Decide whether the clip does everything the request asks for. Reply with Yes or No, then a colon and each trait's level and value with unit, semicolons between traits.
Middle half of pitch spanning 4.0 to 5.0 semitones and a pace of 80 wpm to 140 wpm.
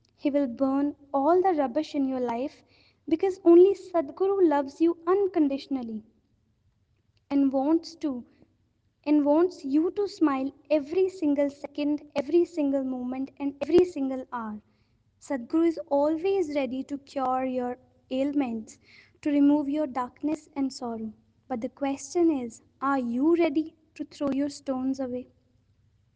No: average, 3.4 semitones; slow, 135 wpm